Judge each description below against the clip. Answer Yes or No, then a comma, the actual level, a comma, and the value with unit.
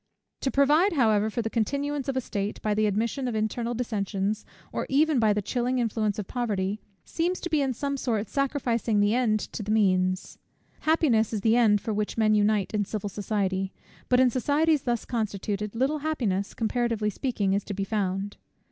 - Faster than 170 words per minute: Yes, average, 190 wpm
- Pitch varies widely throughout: No, average, 3.9 semitones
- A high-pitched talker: Yes, high, 220 Hz